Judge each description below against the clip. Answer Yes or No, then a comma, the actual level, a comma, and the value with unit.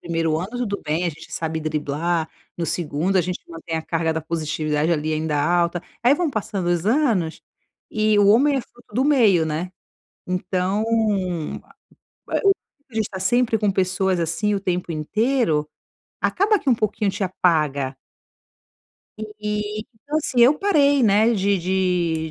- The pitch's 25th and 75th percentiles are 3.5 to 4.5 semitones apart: No, average, 5.1 semitones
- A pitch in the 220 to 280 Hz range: No, medium, 185 Hz